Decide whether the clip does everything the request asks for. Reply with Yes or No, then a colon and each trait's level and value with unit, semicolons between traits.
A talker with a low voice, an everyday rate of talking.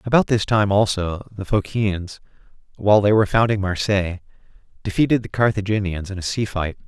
Yes: low, 100 Hz; average, 155 wpm